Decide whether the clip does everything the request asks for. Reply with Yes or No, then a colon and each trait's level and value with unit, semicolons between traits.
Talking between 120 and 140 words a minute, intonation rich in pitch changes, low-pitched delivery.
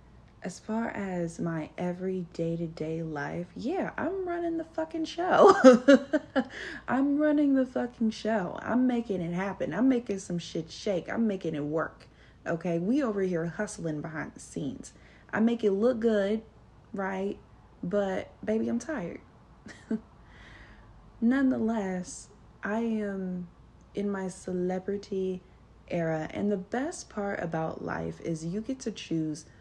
No: slow, 135 wpm; wide, 5.7 semitones; high, 200 Hz